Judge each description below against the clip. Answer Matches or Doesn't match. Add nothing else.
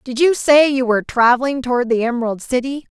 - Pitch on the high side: Matches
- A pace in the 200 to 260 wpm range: Matches